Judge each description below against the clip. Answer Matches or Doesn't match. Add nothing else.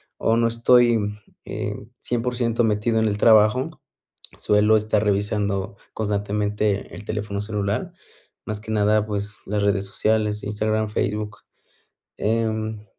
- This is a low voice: Matches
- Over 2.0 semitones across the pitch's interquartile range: Doesn't match